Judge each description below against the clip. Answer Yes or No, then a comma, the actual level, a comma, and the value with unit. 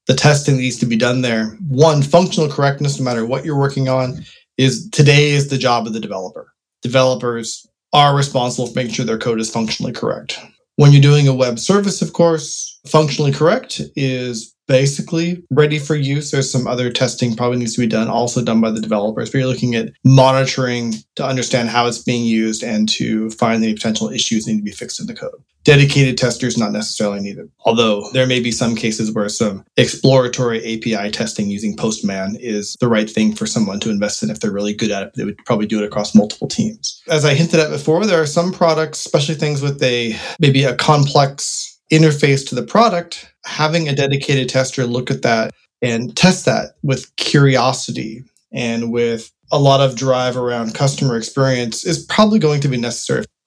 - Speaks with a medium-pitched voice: No, low, 130 Hz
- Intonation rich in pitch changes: No, average, 4.4 semitones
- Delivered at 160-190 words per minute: No, average, 200 wpm